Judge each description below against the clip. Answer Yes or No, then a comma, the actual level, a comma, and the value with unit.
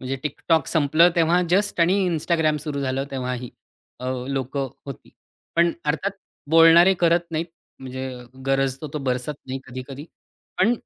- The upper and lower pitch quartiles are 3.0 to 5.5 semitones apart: Yes, average, 4.0 semitones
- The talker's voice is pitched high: No, medium, 150 Hz